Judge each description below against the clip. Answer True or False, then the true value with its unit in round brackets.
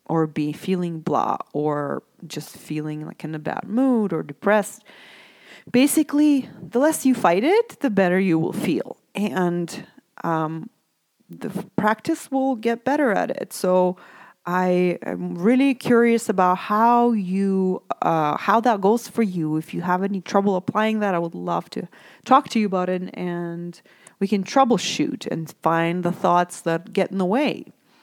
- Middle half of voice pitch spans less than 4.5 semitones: False (5.2 semitones)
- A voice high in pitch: True (195 Hz)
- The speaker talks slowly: False (165 wpm)